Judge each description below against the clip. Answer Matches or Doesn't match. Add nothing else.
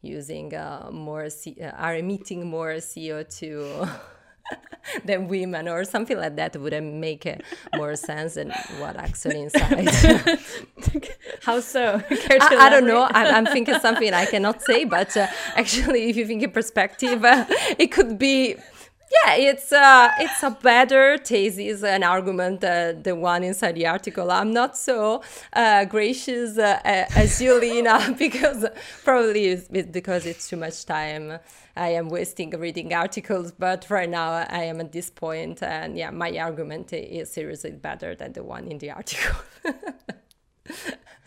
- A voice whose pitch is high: Matches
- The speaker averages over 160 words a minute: Doesn't match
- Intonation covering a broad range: Matches